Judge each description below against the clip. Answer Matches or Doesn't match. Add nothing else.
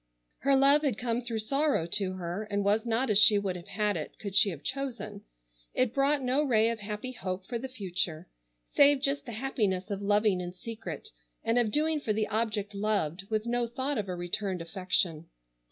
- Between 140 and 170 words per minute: Doesn't match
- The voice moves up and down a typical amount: Matches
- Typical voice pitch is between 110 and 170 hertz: Doesn't match